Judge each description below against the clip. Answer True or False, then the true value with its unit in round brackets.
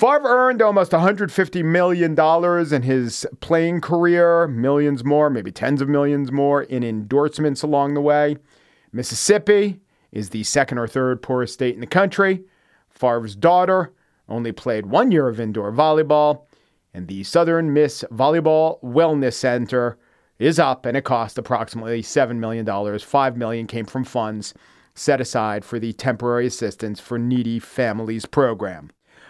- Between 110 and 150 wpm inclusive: True (145 wpm)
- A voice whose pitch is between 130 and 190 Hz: True (135 Hz)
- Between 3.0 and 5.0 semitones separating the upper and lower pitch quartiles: False (5.6 semitones)